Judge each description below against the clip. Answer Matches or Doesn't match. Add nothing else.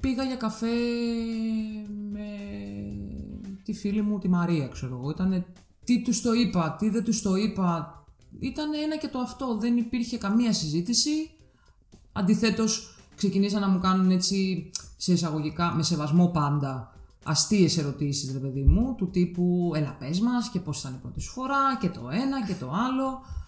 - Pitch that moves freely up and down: Matches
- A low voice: Doesn't match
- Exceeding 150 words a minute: Matches